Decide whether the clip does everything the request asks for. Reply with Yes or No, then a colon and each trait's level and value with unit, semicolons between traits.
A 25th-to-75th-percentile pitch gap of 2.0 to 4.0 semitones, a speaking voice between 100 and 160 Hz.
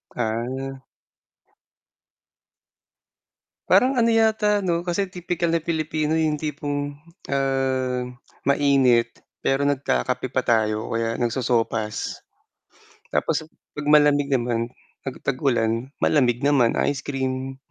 Yes: average, 3.6 semitones; low, 135 Hz